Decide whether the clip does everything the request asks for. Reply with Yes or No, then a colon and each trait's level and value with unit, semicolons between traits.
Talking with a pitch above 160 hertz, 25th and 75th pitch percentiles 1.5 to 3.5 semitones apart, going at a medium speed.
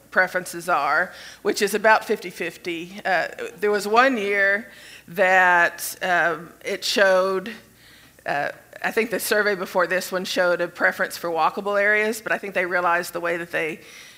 Yes: medium, 185 Hz; average, 2.8 semitones; average, 165 wpm